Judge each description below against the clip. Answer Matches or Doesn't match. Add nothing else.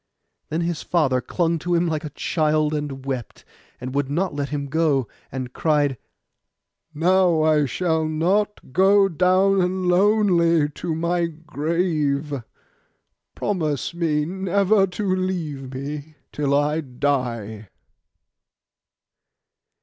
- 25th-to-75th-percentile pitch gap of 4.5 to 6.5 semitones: Doesn't match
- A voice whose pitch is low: Doesn't match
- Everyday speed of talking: Doesn't match